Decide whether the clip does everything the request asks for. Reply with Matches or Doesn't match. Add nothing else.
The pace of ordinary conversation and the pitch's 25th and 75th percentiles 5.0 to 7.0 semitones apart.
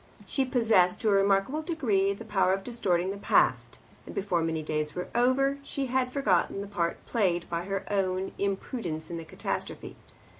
Matches